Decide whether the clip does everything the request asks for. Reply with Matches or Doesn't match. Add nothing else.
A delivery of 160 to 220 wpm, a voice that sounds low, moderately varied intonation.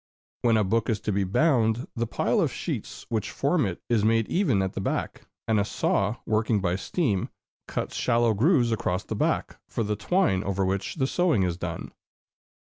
Matches